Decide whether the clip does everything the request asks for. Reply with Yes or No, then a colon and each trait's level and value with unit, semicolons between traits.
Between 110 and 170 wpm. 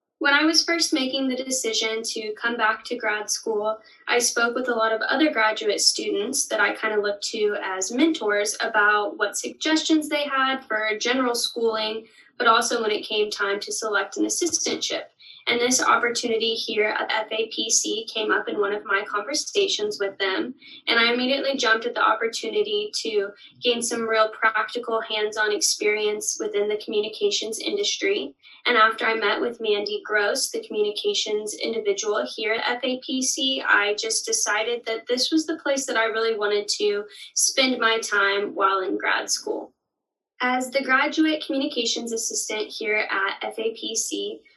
Yes: average, 165 wpm